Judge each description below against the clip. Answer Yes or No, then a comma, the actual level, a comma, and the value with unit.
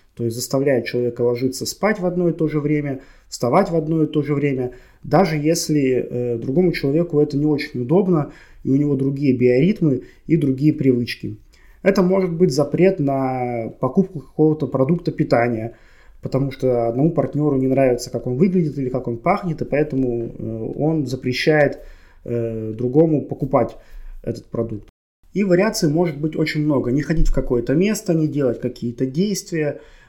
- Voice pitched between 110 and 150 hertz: Yes, medium, 140 Hz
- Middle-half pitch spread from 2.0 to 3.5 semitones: No, average, 4.3 semitones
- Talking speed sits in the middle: No, fast, 165 wpm